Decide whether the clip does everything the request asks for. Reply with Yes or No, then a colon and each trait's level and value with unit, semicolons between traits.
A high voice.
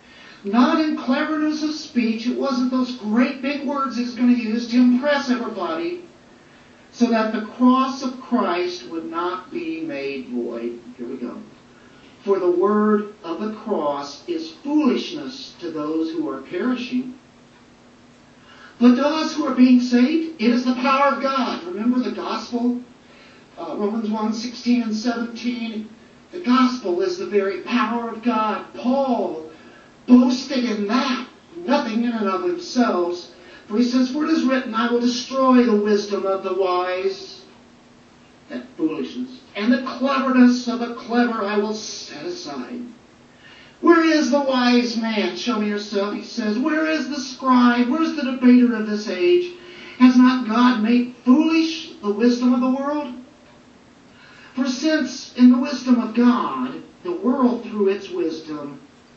Yes: high, 245 Hz